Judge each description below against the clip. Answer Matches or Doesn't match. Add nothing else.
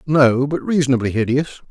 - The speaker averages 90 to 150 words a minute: Matches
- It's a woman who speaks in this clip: Doesn't match